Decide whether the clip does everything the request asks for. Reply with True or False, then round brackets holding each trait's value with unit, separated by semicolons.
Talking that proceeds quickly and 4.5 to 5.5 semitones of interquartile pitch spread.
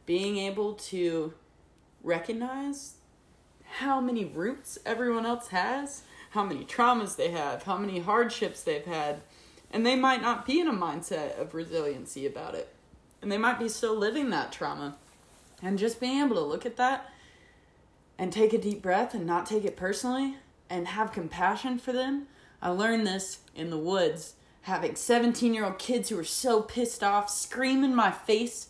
False (175 wpm; 5.2 semitones)